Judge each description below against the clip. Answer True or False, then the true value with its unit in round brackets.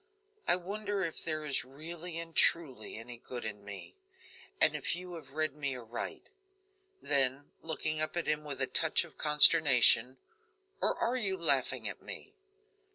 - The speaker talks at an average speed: True (160 wpm)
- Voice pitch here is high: False (155 Hz)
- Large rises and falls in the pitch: False (4.4 semitones)